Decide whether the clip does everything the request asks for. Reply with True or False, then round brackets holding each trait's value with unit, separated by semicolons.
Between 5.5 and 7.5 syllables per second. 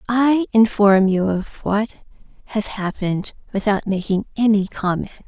False (4.8 syllables/s)